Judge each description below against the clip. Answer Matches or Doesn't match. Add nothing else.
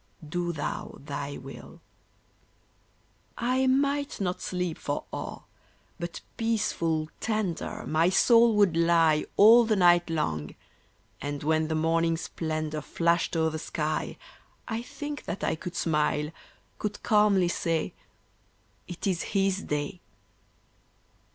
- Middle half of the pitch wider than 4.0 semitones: Matches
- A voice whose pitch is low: Doesn't match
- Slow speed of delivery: Matches